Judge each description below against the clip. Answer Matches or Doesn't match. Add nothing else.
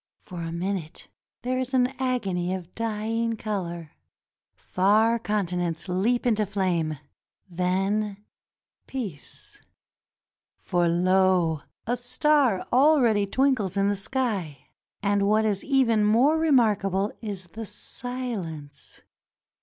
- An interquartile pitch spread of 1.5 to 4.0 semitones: Doesn't match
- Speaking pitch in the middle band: Doesn't match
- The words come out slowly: Matches